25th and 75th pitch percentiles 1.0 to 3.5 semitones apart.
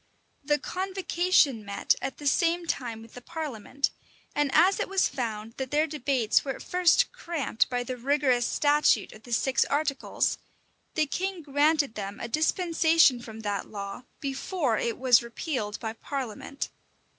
No: average, 5.2 semitones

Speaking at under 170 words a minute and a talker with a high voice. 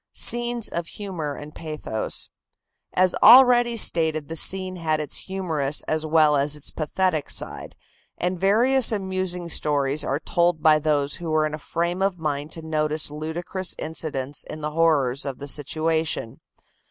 No: average, 155 wpm; medium, 160 Hz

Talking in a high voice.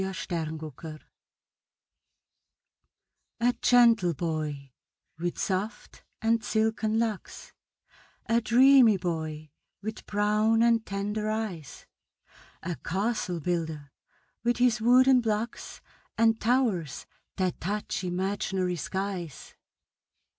Yes: high, 205 Hz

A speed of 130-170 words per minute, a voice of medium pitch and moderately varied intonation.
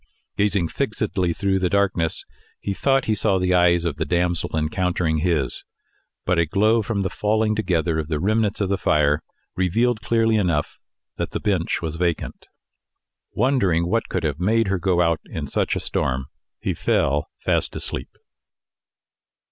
No: average, 165 wpm; very low, 90 Hz; average, 4.2 semitones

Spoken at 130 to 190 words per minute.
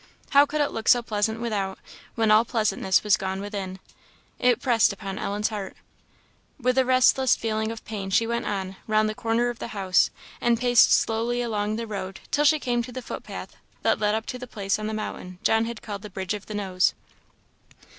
No: fast, 205 wpm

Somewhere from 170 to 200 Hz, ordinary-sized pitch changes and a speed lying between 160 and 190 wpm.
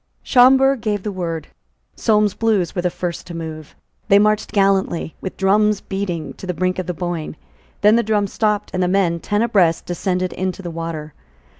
Yes: high, 190 Hz; average, 3.3 semitones; average, 185 wpm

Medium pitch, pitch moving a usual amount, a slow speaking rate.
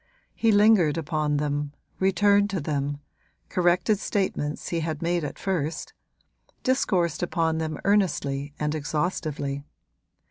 Yes: medium, 160 Hz; average, 4.3 semitones; slow, 115 wpm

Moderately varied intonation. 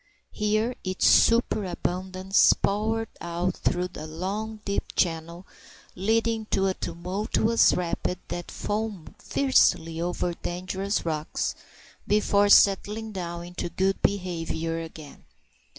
Yes: average, 3.5 semitones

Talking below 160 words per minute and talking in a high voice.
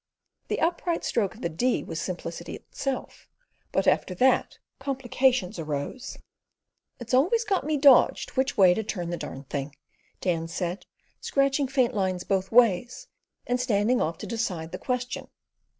Yes: average, 150 wpm; high, 235 Hz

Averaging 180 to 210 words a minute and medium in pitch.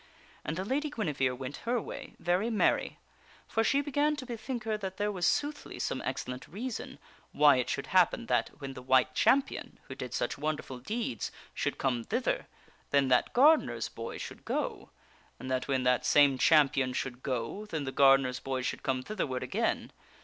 Yes: average, 190 wpm; medium, 145 Hz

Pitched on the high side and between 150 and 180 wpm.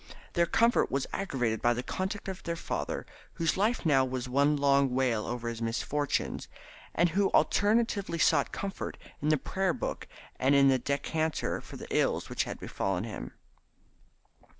No: medium, 145 Hz; average, 165 wpm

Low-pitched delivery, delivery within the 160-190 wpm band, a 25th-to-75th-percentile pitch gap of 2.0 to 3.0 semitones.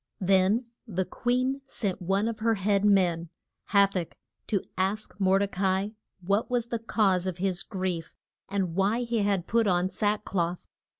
No: high, 195 Hz; average, 175 wpm; narrow, 2.6 semitones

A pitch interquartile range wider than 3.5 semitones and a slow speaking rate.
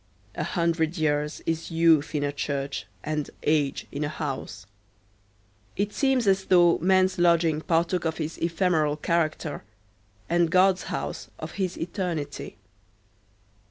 No: average, 3.0 semitones; slow, 130 wpm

